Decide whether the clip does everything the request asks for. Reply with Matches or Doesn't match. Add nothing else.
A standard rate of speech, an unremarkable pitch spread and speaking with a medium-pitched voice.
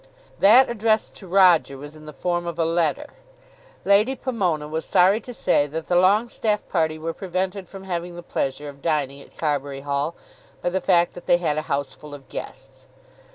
Matches